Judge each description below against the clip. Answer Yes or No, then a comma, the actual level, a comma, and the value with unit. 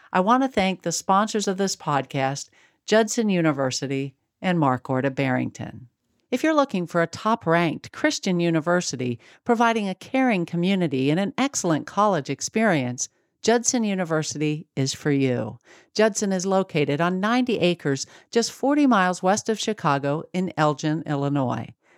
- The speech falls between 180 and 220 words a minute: No, average, 145 wpm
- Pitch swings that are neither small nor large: No, wide, 7.2 semitones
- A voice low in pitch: No, medium, 175 Hz